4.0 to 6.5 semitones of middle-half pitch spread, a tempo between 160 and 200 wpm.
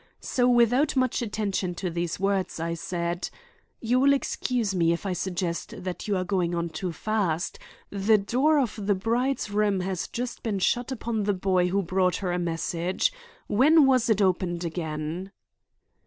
Yes: average, 4.7 semitones; average, 170 wpm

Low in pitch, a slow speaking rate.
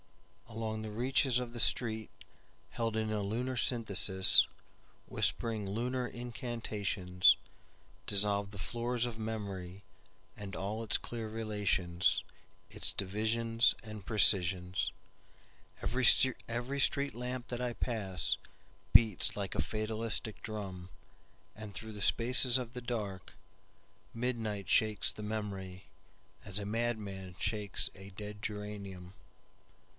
Yes: low, 110 Hz; slow, 95 wpm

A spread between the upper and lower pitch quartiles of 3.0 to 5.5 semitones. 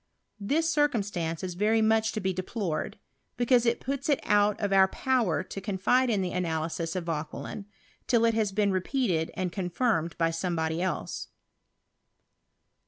Yes: average, 4.7 semitones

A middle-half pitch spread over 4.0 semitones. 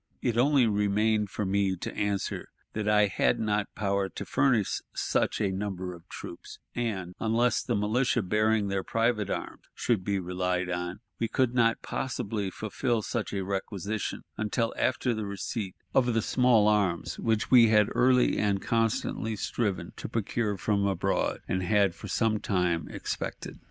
No: average, 2.7 semitones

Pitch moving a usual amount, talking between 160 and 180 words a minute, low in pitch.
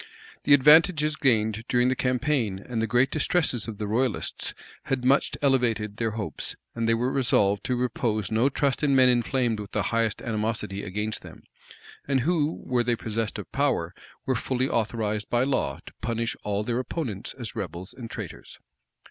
Yes: average, 3.5 semitones; average, 175 wpm; low, 120 Hz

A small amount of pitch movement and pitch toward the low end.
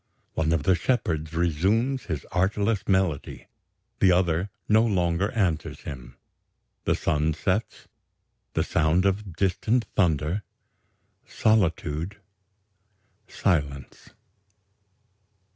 No: average, 4.1 semitones; very low, 90 Hz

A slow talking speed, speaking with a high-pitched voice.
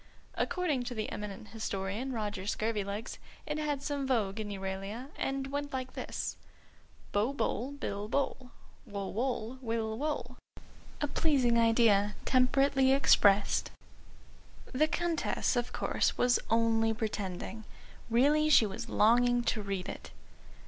Yes: slow, 130 wpm; high, 235 Hz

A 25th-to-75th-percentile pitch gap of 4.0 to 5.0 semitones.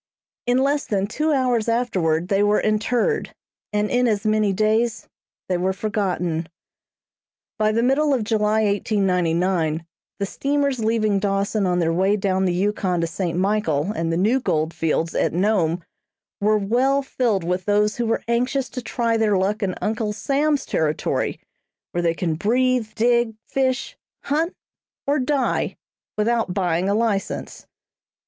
Yes: average, 4.5 semitones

